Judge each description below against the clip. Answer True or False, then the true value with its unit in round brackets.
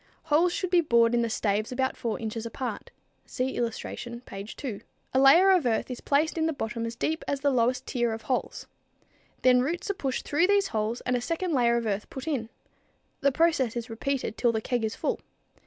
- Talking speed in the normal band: False (215 wpm)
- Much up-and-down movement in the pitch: False (4.2 semitones)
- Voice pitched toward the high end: True (250 Hz)